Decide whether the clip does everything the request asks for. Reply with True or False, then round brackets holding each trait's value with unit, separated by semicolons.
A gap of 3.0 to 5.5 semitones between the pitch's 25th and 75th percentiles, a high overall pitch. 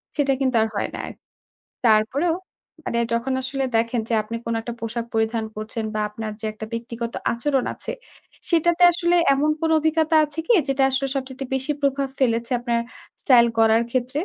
True (3.4 semitones; 250 Hz)